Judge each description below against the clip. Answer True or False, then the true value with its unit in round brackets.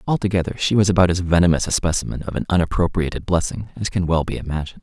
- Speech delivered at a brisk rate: True (210 wpm)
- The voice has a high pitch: False (90 Hz)